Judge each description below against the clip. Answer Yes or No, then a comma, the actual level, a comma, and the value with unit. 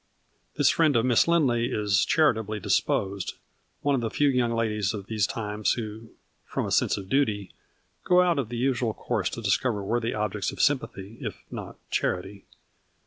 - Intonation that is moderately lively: Yes, average, 3.9 semitones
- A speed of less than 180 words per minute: No, average, 185 wpm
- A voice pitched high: No, low, 115 Hz